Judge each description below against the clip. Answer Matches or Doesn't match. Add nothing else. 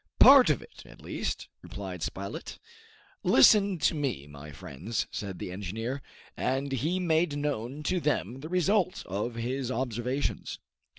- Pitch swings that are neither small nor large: Doesn't match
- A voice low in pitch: Matches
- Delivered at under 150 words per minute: Matches